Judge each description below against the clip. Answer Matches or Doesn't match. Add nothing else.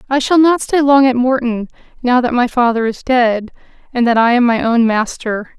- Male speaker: Doesn't match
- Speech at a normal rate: Doesn't match